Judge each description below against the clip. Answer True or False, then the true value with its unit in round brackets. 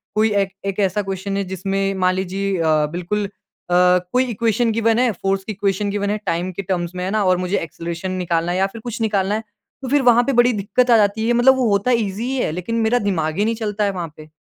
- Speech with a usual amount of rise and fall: True (3.3 semitones)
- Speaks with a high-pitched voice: True (200 Hz)